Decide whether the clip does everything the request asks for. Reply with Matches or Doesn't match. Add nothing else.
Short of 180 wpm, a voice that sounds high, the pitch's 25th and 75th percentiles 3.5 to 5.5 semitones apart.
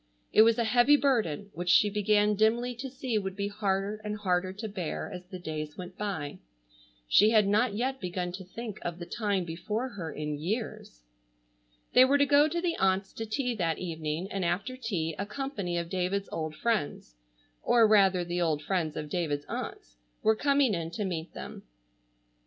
Doesn't match